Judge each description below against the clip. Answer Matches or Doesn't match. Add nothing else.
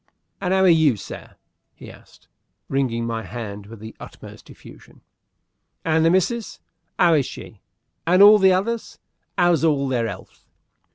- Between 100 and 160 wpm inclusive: Matches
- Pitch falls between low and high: Matches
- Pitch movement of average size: Doesn't match